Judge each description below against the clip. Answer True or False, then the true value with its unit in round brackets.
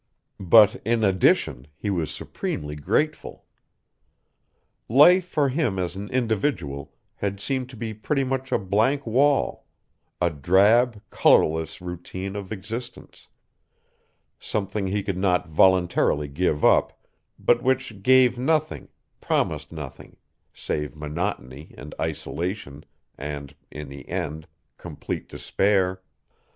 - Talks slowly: True (115 wpm)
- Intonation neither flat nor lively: False (7.1 semitones)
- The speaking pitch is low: True (95 Hz)